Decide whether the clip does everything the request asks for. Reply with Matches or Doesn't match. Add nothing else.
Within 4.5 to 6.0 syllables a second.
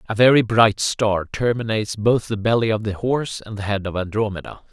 Matches